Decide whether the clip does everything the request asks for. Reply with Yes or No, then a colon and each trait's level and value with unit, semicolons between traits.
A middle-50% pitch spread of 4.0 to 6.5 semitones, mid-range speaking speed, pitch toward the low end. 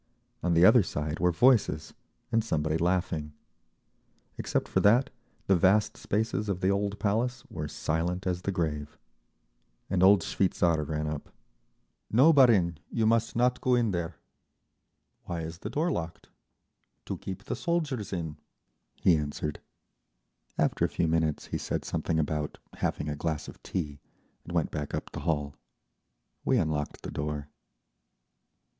Yes: wide, 5.5 semitones; average, 150 wpm; very low, 90 Hz